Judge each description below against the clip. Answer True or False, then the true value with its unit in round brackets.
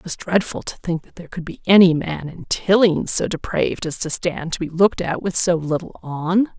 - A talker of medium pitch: True (170 Hz)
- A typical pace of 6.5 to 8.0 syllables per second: False (5.4 syllables/s)